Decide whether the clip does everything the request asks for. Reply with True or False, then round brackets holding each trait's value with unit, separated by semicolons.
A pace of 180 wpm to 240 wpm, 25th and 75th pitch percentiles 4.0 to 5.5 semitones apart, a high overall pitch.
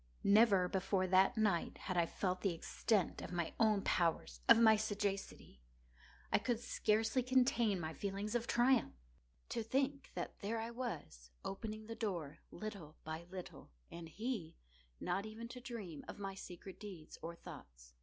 False (155 wpm; 4.5 semitones; 200 Hz)